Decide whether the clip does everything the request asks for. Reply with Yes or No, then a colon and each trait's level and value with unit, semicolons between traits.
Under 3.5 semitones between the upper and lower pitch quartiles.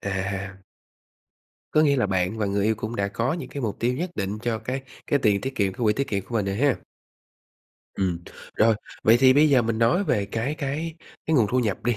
No: average, 5.1 semitones